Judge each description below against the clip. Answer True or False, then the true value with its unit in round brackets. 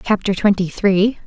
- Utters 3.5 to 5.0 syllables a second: True (4.5 syllables/s)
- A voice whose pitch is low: False (195 Hz)